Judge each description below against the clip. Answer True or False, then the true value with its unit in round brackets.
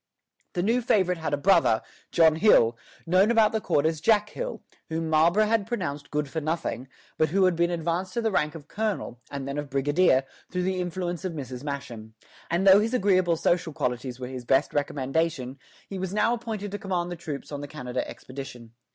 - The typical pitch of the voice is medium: True (165 Hz)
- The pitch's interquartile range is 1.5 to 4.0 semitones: False (5.4 semitones)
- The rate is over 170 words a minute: True (205 wpm)